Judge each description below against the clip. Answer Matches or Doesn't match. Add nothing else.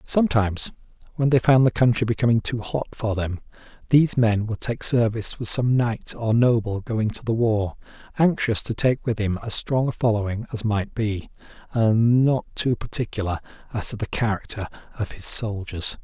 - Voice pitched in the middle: Doesn't match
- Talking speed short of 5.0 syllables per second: Doesn't match